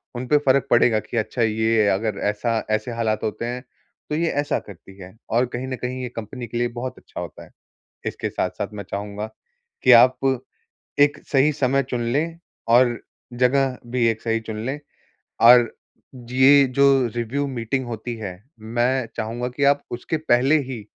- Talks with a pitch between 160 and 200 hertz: No, low, 120 Hz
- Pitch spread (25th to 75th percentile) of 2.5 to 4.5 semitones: Yes, average, 2.8 semitones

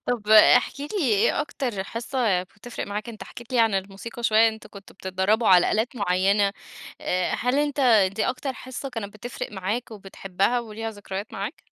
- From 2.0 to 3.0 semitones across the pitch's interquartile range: No, average, 3.6 semitones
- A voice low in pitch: No, high, 220 Hz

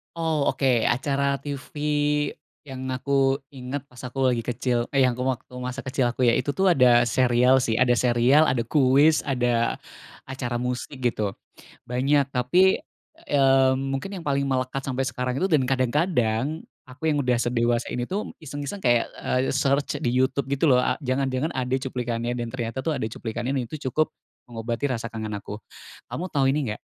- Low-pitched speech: Yes, low, 130 Hz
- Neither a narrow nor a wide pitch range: No, narrow, 2.2 semitones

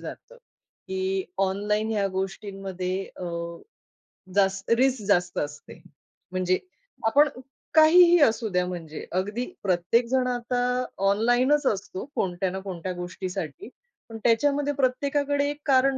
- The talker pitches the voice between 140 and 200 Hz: No, high, 210 Hz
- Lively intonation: Yes, wide, 5.7 semitones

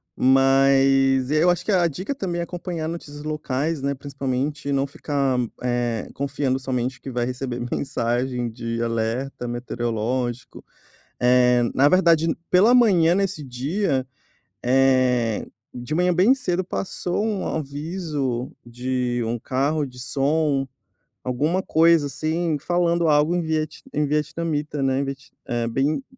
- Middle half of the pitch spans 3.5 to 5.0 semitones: Yes, average, 4.4 semitones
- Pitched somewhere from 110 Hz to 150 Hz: Yes, medium, 140 Hz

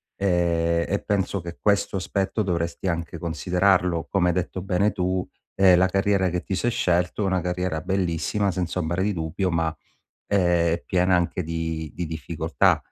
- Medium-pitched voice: No, very low, 90 Hz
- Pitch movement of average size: No, narrow, 2.2 semitones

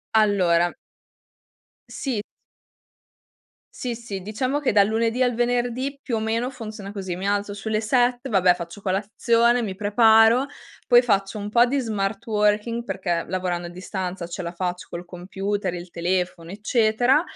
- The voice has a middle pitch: No, high, 210 Hz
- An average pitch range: Yes, average, 4.2 semitones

